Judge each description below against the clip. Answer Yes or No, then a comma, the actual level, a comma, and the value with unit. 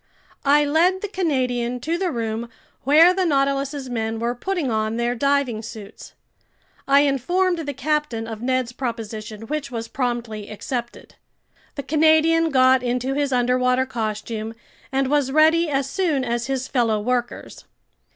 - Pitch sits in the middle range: No, very high, 260 Hz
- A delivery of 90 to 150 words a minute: Yes, average, 145 wpm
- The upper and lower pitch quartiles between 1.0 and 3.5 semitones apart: No, average, 4.0 semitones